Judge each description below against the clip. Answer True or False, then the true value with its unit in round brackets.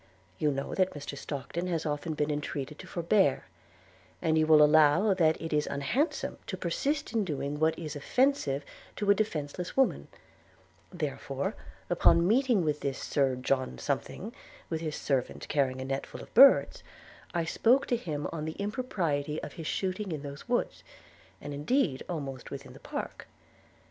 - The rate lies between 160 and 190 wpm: True (165 wpm)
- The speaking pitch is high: False (155 Hz)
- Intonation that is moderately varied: True (5.0 semitones)